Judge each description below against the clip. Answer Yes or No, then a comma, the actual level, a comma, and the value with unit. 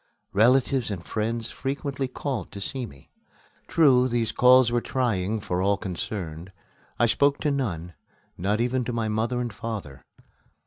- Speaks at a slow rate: No, average, 150 wpm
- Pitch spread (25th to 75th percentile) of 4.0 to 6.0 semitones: Yes, average, 4.4 semitones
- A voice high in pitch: No, low, 115 Hz